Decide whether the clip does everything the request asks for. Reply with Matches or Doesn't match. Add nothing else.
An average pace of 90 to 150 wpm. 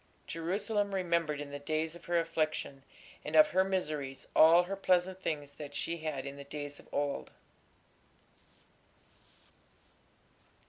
Matches